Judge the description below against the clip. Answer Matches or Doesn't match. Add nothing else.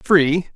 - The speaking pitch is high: Doesn't match